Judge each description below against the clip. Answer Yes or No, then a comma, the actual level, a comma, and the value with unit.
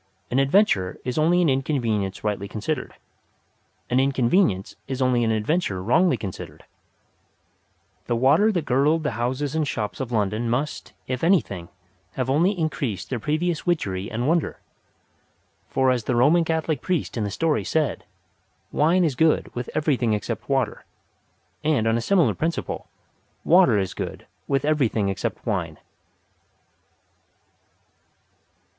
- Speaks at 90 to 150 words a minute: Yes, average, 140 wpm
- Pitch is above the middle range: No, low, 130 Hz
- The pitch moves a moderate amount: No, wide, 6.1 semitones